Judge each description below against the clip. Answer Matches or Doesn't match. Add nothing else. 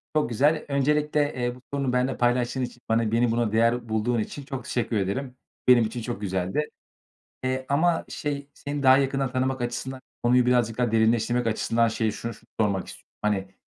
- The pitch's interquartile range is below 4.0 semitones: Matches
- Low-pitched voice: Matches